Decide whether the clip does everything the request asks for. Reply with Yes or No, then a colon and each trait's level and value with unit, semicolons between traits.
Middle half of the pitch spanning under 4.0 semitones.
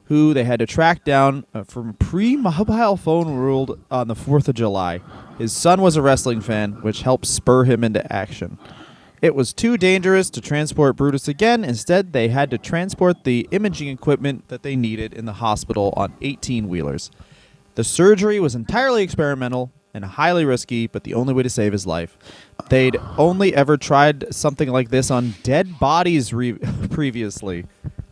No: average, 5.2 semitones